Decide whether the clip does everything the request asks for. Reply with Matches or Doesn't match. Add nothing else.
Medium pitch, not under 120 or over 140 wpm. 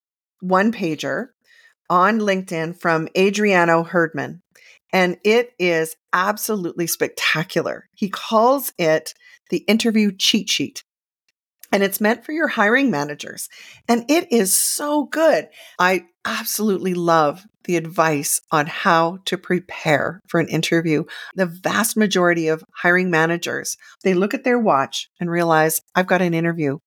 Matches